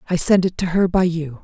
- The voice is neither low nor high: Yes, medium, 175 Hz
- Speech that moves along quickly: Yes, fast, 295 wpm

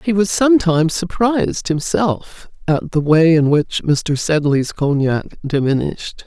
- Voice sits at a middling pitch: Yes, medium, 165 Hz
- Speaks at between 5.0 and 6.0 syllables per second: No, 4.2 syllables/s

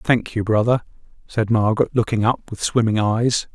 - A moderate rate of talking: Yes, average, 170 wpm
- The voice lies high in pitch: No, low, 110 Hz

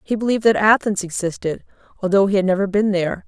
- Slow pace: No, average, 200 wpm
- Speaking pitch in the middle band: No, high, 200 Hz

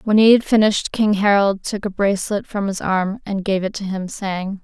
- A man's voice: No, female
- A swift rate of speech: Yes, fast, 235 wpm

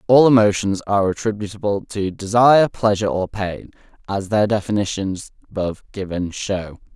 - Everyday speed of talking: No, slow, 130 wpm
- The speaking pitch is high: No, low, 100 Hz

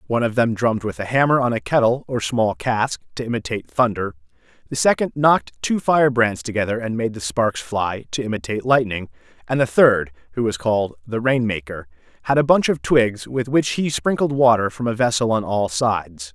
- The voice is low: Yes, low, 115 Hz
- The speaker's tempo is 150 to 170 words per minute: No, fast, 205 wpm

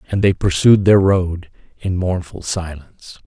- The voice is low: Yes, very low, 90 Hz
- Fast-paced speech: No, average, 145 wpm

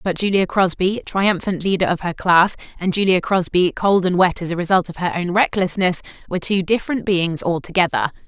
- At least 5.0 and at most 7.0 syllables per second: Yes, 5.5 syllables/s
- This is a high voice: No, medium, 180 Hz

